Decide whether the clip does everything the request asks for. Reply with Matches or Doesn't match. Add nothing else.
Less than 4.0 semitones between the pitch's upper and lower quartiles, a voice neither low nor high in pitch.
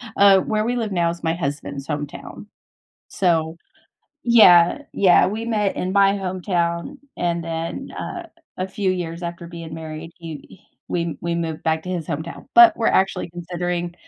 Matches